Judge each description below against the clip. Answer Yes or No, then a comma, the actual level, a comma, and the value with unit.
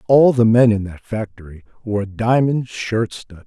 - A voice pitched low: Yes, low, 110 Hz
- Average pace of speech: Yes, average, 175 wpm